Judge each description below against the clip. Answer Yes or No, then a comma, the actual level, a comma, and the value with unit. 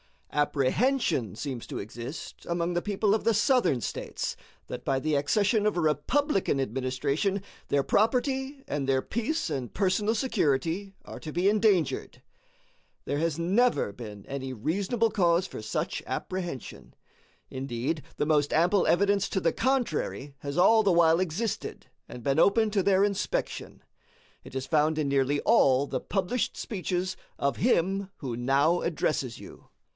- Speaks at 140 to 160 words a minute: Yes, average, 150 wpm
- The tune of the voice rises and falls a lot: Yes, wide, 6.6 semitones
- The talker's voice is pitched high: No, medium, 170 Hz